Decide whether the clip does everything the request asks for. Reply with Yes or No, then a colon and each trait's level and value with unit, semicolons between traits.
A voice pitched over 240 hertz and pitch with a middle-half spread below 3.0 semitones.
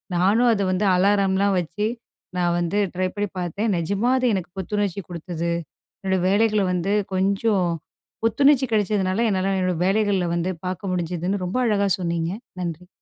No: high, 190 Hz; narrow, 2.6 semitones